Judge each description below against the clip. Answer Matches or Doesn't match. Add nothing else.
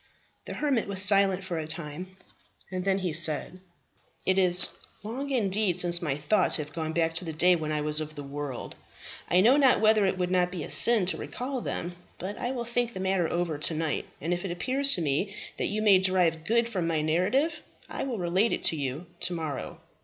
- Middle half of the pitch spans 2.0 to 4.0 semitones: Doesn't match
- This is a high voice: Doesn't match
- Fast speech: Matches